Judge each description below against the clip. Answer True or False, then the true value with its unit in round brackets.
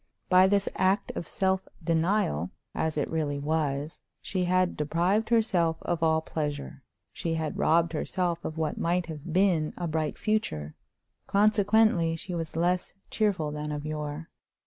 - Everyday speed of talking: True (150 wpm)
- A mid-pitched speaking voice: True (165 Hz)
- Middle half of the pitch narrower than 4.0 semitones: True (3.3 semitones)